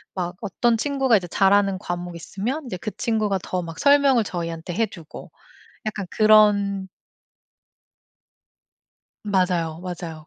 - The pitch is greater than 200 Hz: No, high, 195 Hz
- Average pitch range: Yes, average, 3.6 semitones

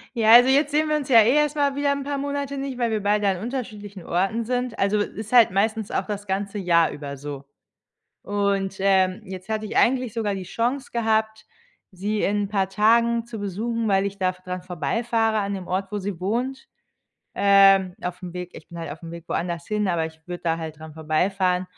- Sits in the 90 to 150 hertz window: No, high, 205 Hz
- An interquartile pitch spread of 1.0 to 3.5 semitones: No, average, 4.0 semitones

